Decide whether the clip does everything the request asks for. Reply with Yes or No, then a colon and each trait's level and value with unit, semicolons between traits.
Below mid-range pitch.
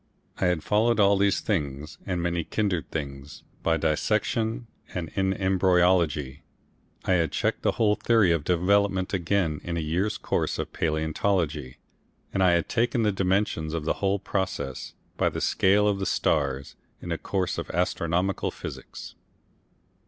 Yes: very low, 90 Hz